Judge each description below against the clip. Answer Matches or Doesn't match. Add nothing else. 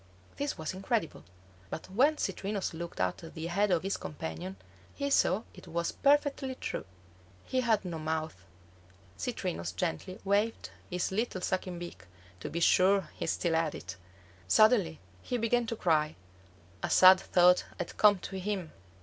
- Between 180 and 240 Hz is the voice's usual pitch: Matches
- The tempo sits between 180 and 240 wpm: Doesn't match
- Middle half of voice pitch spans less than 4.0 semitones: Doesn't match